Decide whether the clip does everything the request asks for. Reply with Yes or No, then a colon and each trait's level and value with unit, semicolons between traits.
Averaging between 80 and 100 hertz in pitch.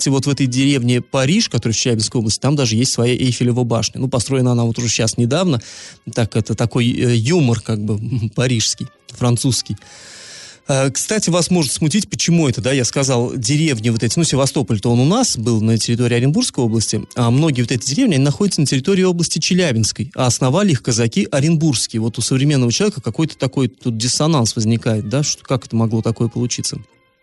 No: low, 125 Hz